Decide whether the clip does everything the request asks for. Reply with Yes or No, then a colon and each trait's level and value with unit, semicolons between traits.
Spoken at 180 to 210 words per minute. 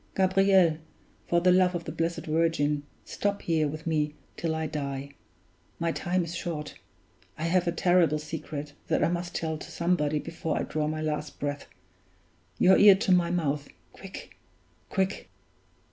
No: average, 160 wpm